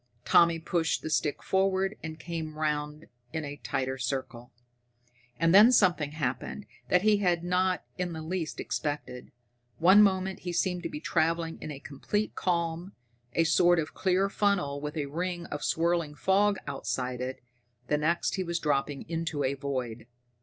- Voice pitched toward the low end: No, medium, 165 Hz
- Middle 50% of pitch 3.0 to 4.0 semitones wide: Yes, average, 3.6 semitones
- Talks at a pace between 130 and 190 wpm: Yes, average, 165 wpm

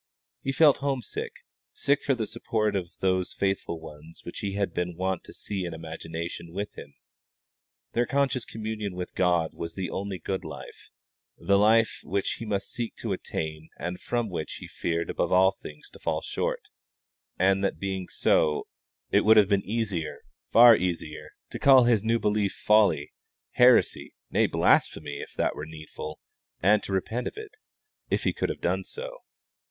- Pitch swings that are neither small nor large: Yes, average, 4.5 semitones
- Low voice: Yes, very low, 95 Hz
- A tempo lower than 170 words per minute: No, average, 175 wpm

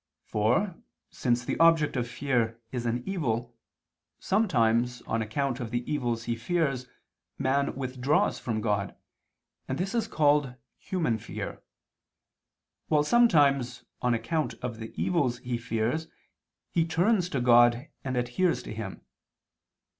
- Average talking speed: No, slow, 130 wpm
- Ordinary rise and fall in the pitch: Yes, average, 4.9 semitones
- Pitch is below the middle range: Yes, low, 125 Hz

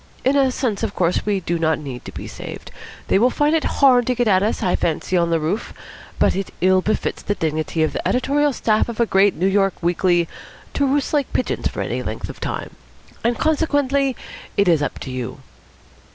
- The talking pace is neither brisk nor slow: No, fast, 215 wpm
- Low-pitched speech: No, high, 200 Hz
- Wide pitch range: Yes, wide, 7.1 semitones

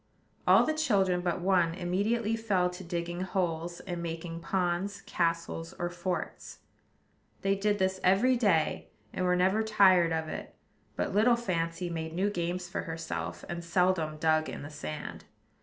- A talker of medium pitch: Yes, medium, 180 Hz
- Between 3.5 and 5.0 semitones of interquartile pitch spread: No, average, 2.7 semitones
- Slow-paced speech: No, average, 155 wpm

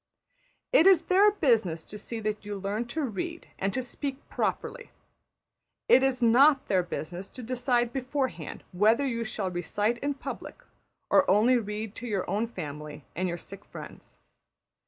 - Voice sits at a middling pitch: No, high, 230 Hz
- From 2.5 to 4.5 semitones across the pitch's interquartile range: No, average, 5.1 semitones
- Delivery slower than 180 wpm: Yes, average, 160 wpm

